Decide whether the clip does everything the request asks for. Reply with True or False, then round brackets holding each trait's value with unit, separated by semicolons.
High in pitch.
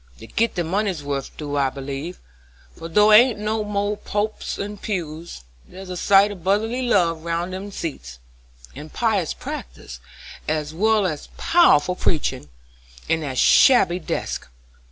False (180 Hz)